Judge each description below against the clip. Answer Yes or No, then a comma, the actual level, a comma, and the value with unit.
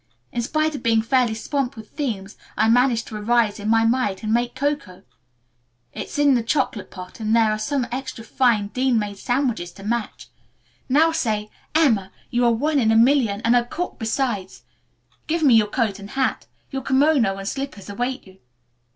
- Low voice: No, high, 235 Hz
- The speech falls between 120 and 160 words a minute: No, average, 185 wpm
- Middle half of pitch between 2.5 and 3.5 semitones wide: No, average, 3.9 semitones